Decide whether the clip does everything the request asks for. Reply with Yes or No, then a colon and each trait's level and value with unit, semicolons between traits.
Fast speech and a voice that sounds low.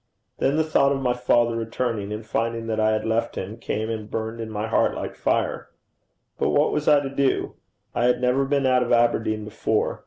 Yes: fast, 215 wpm; low, 115 Hz